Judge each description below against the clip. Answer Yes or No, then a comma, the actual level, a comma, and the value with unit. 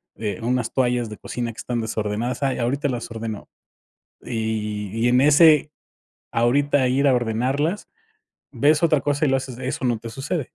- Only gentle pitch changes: No, average, 3.6 semitones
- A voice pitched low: Yes, low, 125 Hz